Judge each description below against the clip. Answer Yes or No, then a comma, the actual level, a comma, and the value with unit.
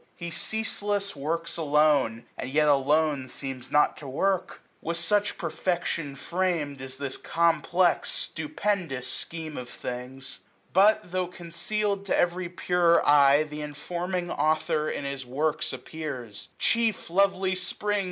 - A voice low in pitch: No, medium, 165 Hz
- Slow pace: Yes, slow, 130 wpm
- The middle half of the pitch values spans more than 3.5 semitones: Yes, average, 4.3 semitones